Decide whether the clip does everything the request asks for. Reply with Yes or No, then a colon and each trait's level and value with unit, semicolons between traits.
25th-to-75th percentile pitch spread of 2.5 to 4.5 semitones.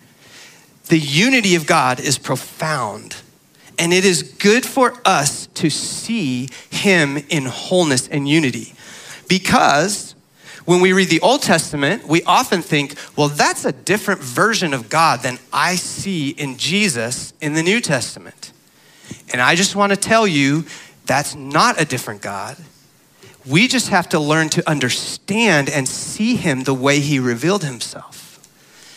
No: wide, 5.4 semitones